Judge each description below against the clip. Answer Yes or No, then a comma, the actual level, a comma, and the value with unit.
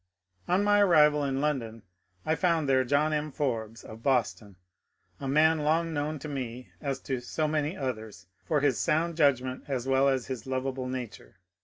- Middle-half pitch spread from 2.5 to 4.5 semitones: Yes, average, 3.1 semitones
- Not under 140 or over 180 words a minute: Yes, average, 175 wpm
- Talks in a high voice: No, medium, 140 Hz